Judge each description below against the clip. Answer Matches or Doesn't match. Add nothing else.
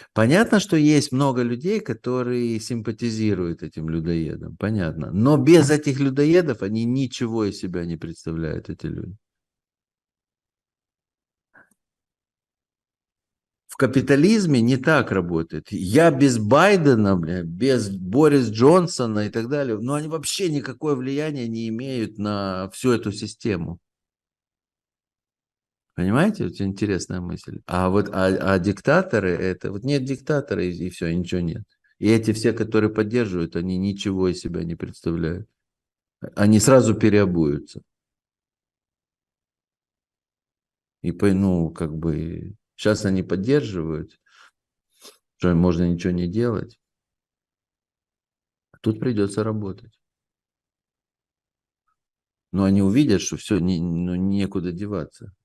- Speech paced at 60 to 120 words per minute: Matches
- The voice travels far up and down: Matches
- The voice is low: Matches